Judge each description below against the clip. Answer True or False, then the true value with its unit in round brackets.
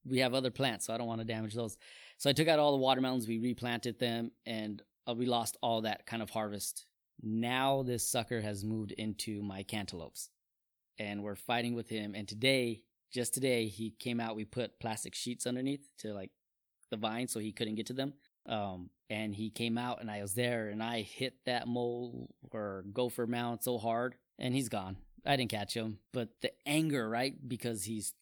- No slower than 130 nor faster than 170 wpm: False (205 wpm)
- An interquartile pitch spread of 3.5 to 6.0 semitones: False (2.5 semitones)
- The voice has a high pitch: False (115 Hz)